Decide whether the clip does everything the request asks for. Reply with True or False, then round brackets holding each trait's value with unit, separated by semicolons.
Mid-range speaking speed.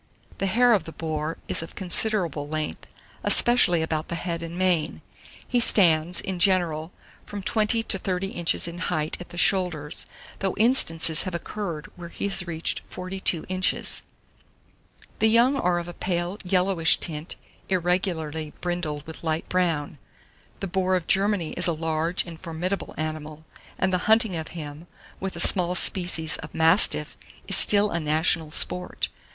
True (160 wpm)